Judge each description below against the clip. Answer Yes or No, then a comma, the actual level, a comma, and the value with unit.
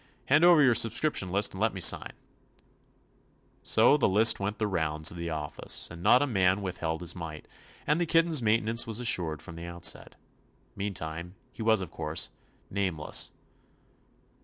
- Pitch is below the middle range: Yes, low, 100 Hz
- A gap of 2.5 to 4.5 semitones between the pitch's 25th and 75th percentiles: No, average, 5.2 semitones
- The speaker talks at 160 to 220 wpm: Yes, average, 170 wpm